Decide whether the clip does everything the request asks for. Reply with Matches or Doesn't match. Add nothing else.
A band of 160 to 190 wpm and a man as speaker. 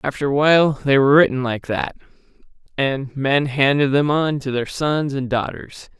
Matches